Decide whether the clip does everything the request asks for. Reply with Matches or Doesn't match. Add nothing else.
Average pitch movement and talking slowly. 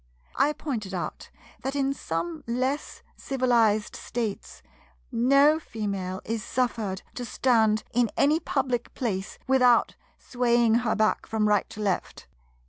Matches